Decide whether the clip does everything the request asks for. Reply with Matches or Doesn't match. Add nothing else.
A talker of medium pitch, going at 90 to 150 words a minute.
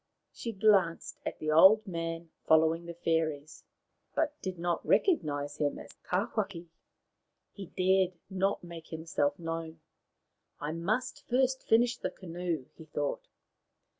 Matches